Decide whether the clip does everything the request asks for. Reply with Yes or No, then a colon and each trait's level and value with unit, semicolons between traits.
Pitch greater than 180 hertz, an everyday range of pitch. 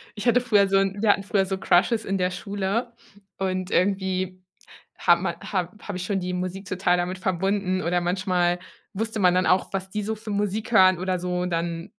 No: high, 190 Hz; narrow, 1.9 semitones